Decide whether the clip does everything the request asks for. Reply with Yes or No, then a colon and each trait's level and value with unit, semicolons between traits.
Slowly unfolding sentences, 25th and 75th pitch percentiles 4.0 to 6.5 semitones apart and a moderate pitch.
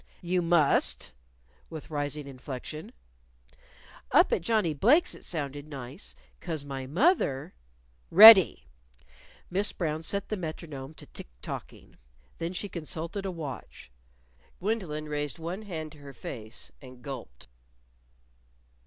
Yes: slow, 125 wpm; average, 4.5 semitones; medium, 155 Hz